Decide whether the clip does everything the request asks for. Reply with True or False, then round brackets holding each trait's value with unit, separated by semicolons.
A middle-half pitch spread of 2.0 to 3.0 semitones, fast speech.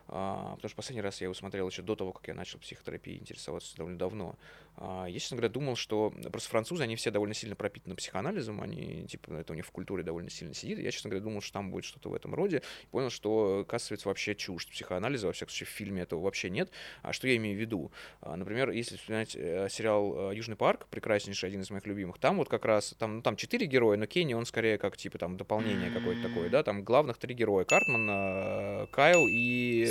True (2.7 semitones; 230 wpm)